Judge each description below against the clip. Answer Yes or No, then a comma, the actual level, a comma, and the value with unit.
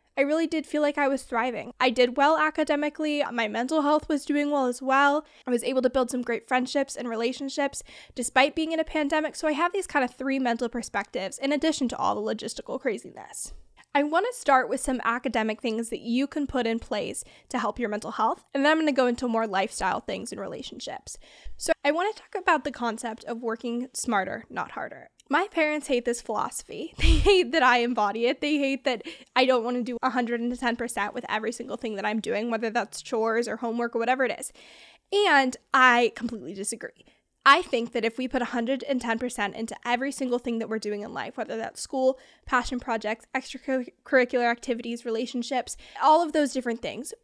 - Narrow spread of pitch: No, average, 3.4 semitones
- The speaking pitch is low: No, very high, 255 Hz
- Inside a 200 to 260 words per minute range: Yes, fast, 205 wpm